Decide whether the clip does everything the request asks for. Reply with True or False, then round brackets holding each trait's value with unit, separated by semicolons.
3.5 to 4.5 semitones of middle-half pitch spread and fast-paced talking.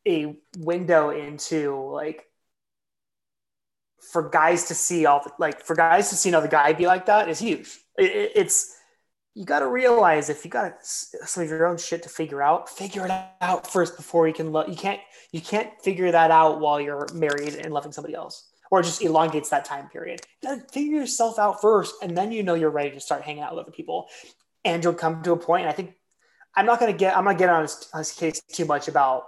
True (4.0 semitones; 230 wpm)